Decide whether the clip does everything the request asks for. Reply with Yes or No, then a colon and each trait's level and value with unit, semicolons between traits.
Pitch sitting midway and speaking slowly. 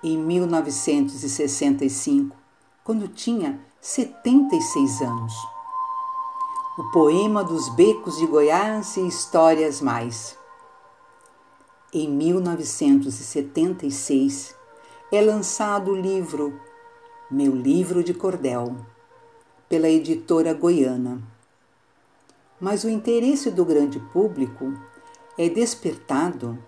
Yes: medium, 180 Hz; slow, 80 wpm